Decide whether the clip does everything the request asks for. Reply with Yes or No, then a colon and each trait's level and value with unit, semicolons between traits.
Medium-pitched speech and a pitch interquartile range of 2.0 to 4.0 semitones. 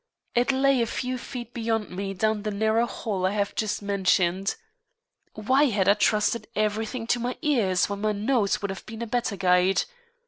No: high, 215 Hz; average, 3.0 semitones